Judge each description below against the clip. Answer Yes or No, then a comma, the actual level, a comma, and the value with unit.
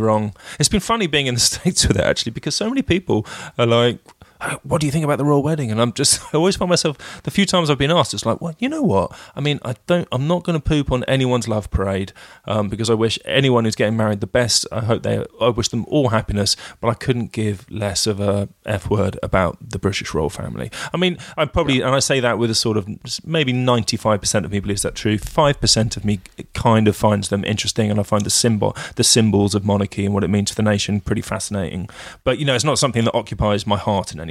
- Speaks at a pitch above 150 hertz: No, low, 115 Hz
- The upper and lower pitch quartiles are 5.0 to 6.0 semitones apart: Yes, wide, 5.4 semitones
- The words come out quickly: Yes, fast, 255 wpm